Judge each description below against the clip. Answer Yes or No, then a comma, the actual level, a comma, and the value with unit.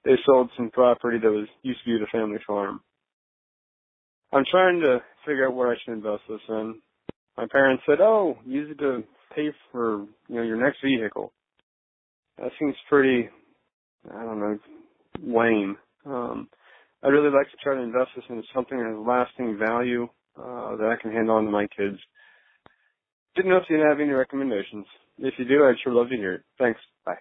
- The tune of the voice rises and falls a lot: No, average, 3.9 semitones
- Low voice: Yes, low, 125 Hz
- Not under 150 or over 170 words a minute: No, average, 190 wpm